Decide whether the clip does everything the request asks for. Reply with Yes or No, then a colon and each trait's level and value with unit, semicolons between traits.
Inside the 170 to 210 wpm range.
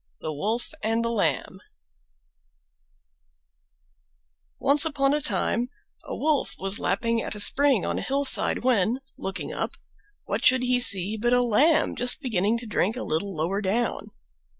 No: average, 150 wpm